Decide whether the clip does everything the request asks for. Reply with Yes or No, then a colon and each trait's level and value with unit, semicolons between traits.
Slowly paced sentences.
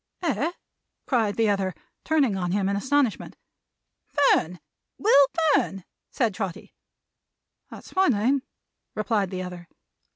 Yes: slow, 120 wpm